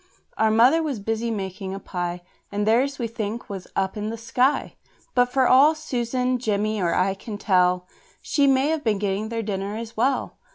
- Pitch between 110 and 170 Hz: No, high, 220 Hz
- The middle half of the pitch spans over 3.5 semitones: Yes, average, 4.1 semitones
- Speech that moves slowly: No, average, 195 wpm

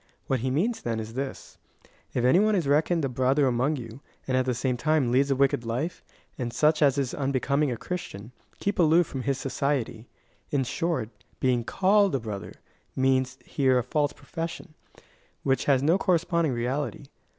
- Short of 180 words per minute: No, average, 185 wpm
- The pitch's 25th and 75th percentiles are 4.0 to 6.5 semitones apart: No, average, 3.6 semitones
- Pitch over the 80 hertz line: Yes, low, 135 Hz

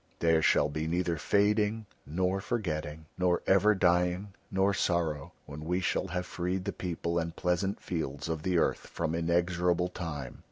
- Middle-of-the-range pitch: No, very low, 90 Hz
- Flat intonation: Yes, narrow, 2.3 semitones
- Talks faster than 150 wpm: Yes, average, 160 wpm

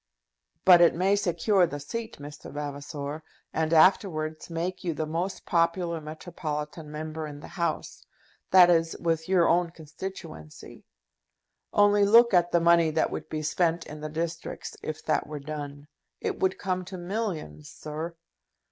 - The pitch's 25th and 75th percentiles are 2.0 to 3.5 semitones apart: Yes, average, 2.8 semitones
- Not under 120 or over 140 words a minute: No, average, 155 wpm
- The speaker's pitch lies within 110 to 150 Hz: No, medium, 165 Hz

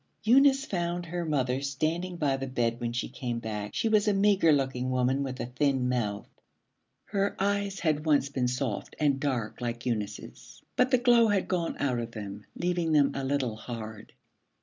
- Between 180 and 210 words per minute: Yes, average, 185 wpm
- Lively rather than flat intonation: Yes, wide, 6.3 semitones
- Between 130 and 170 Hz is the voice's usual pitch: Yes, medium, 140 Hz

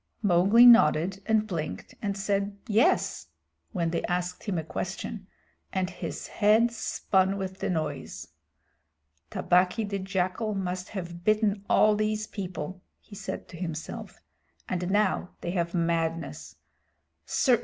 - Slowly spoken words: Yes, slow, 130 wpm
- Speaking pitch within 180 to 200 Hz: Yes, high, 190 Hz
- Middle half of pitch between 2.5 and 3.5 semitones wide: Yes, average, 2.9 semitones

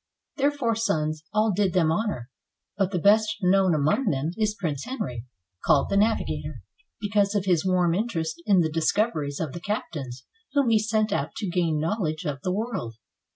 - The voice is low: No, medium, 185 Hz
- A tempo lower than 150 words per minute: No, average, 180 wpm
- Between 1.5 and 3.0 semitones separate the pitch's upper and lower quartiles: No, wide, 5.6 semitones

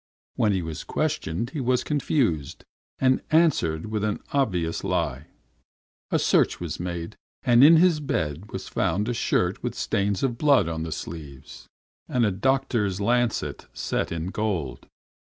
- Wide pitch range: Yes, wide, 7.6 semitones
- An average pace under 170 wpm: Yes, average, 150 wpm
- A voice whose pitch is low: Yes, low, 105 Hz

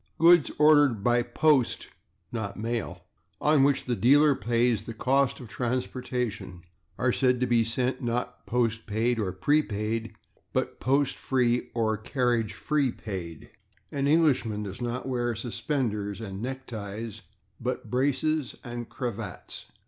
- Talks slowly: Yes, slow, 130 wpm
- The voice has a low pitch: Yes, low, 120 Hz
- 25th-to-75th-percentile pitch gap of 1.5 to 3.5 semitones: Yes, average, 3.0 semitones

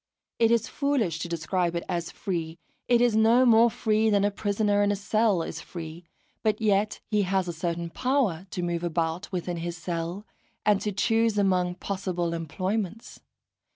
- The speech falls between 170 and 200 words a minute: Yes, average, 175 wpm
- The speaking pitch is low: No, high, 195 Hz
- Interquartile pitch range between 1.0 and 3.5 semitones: No, average, 3.9 semitones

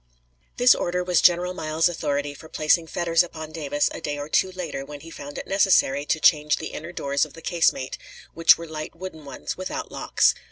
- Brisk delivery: Yes, fast, 210 wpm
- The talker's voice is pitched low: No, medium, 160 Hz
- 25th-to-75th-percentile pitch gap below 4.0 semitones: Yes, average, 3.1 semitones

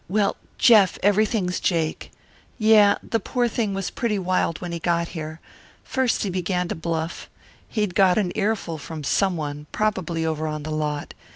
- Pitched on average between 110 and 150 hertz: No, medium, 180 Hz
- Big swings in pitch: No, average, 4.5 semitones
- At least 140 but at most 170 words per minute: Yes, average, 165 wpm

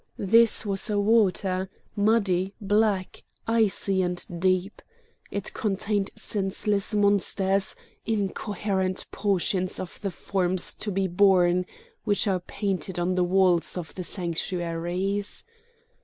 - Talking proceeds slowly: Yes, slow, 110 wpm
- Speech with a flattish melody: Yes, narrow, 1.9 semitones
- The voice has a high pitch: Yes, high, 195 Hz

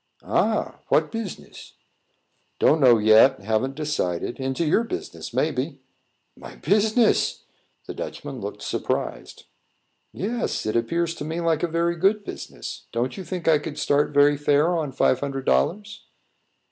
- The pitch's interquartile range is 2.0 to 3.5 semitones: No, average, 5.0 semitones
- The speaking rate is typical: Yes, average, 145 wpm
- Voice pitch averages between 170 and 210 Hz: No, medium, 155 Hz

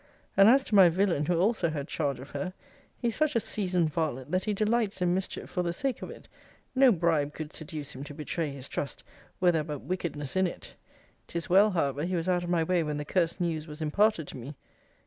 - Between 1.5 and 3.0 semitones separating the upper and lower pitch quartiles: No, average, 4.0 semitones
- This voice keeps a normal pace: No, fast, 235 wpm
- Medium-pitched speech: Yes, medium, 170 Hz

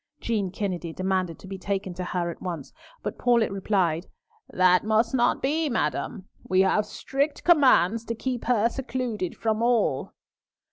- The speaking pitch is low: No, high, 210 Hz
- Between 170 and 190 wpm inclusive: No, average, 155 wpm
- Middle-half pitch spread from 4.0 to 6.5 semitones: Yes, average, 4.6 semitones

